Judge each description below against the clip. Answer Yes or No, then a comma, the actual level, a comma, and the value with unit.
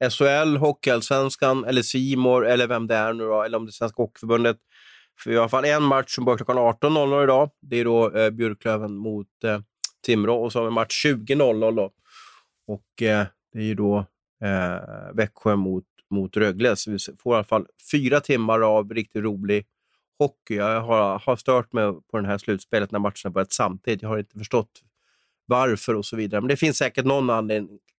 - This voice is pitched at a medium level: No, low, 115 Hz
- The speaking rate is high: Yes, fast, 205 wpm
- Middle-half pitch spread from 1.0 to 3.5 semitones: Yes, average, 3.2 semitones